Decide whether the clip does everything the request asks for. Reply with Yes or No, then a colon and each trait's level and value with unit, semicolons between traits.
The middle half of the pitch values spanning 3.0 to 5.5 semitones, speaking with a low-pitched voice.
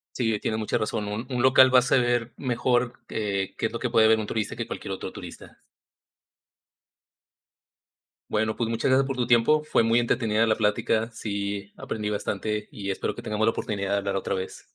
No: narrow, 2.6 semitones; low, 110 Hz